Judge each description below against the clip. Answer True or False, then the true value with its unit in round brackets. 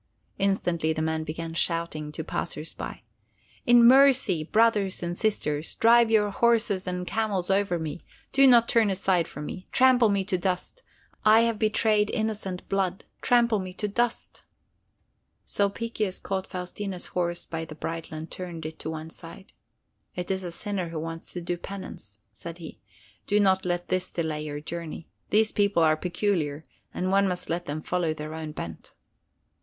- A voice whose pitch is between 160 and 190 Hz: True (185 Hz)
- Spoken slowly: False (170 wpm)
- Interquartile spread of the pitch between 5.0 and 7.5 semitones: False (4.1 semitones)